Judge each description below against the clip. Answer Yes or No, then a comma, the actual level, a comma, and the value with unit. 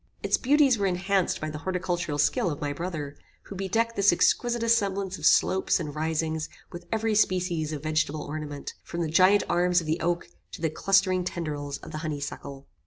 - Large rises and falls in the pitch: No, average, 3.8 semitones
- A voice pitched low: No, medium, 175 Hz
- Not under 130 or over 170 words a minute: No, average, 190 wpm